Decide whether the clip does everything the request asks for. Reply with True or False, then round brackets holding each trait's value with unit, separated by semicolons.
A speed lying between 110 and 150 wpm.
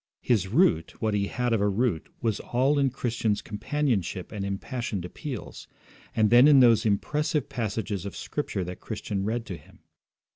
False (170 wpm)